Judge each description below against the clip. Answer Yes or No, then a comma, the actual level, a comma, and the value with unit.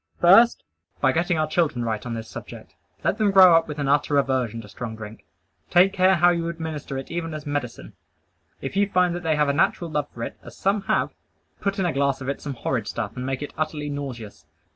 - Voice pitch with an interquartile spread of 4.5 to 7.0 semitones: Yes, average, 4.8 semitones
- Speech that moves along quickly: Yes, fast, 230 wpm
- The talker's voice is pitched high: No, medium, 150 Hz